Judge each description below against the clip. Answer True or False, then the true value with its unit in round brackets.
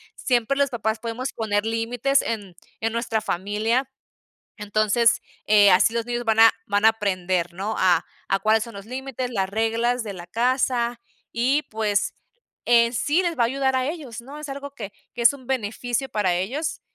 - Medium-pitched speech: False (230 Hz)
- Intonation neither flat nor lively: True (3.3 semitones)